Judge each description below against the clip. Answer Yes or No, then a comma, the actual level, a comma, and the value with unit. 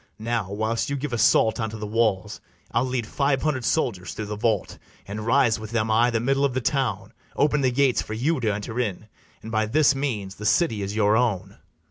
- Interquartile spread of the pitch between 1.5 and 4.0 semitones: Yes, average, 3.5 semitones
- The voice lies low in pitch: Yes, low, 115 Hz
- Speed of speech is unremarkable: No, fast, 215 wpm